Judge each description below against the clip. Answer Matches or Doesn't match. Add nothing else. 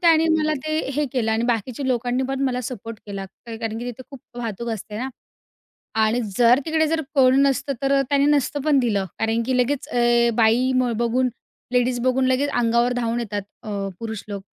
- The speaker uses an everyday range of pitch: Matches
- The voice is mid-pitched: Doesn't match